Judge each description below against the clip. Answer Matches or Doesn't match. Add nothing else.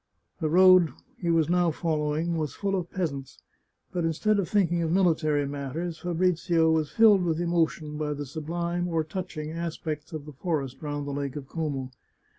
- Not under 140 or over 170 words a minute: Doesn't match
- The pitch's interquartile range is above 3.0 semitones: Doesn't match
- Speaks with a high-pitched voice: Doesn't match